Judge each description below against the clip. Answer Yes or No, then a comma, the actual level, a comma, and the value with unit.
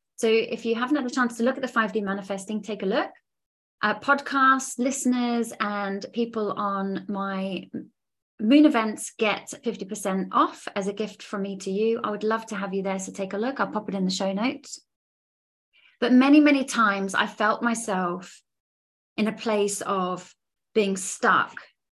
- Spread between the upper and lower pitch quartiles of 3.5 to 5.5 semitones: Yes, average, 3.8 semitones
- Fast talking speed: No, average, 185 wpm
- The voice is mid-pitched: No, high, 215 Hz